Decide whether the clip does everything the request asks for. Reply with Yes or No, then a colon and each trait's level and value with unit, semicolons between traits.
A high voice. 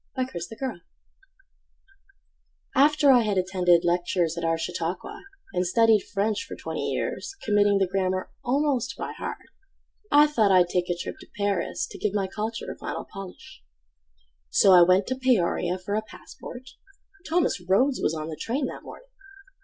Yes: high, 200 Hz